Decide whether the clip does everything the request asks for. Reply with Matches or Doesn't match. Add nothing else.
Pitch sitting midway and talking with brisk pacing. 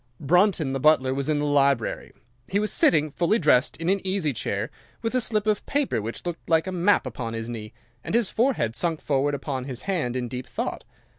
Matches